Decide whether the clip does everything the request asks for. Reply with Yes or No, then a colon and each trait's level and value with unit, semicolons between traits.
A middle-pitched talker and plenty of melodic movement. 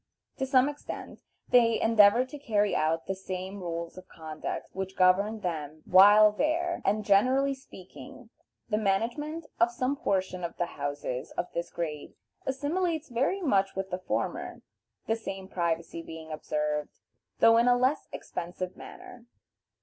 No: high, 200 Hz; wide, 6.4 semitones